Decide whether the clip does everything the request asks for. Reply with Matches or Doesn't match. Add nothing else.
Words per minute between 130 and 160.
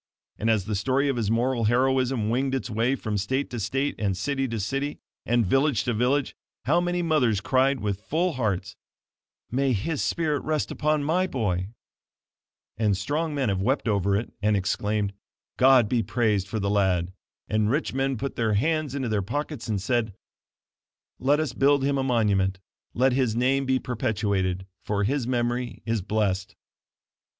Doesn't match